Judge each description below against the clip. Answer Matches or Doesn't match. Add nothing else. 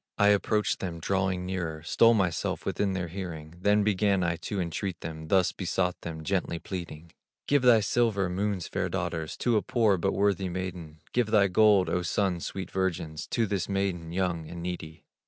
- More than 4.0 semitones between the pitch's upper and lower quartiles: Doesn't match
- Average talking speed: Matches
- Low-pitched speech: Matches